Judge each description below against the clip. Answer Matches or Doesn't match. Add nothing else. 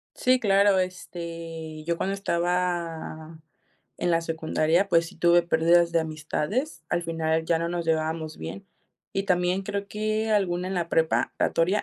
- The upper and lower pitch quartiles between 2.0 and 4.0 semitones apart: Matches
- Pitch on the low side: Doesn't match